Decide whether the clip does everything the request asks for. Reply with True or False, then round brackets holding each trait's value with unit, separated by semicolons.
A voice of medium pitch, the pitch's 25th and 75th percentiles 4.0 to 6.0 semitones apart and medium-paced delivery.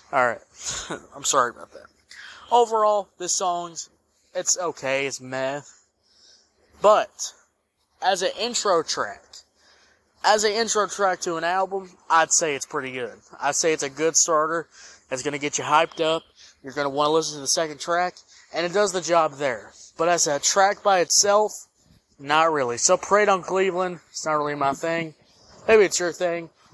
True (165 Hz; 4.3 semitones; 175 wpm)